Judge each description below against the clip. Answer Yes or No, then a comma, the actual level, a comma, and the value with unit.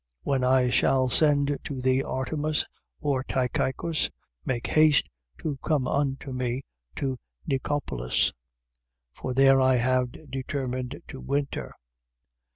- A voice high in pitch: No, low, 135 Hz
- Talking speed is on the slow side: Yes, slow, 115 wpm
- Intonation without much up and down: Yes, narrow, 1.9 semitones